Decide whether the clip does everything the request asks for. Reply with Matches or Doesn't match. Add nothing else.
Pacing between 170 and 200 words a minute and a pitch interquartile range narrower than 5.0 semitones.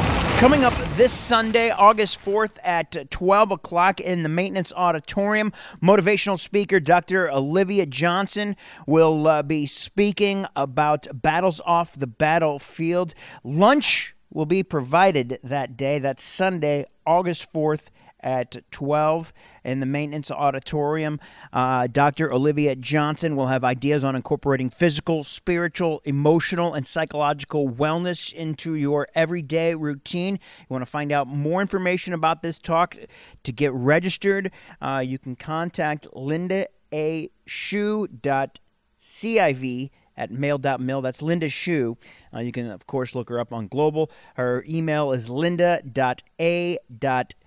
Doesn't match